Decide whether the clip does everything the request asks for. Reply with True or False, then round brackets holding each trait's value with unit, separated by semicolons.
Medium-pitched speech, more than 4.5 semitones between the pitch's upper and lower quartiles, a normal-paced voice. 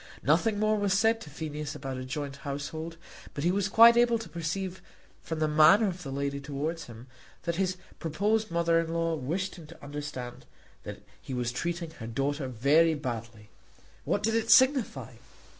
True (160 Hz; 5.5 semitones; 180 wpm)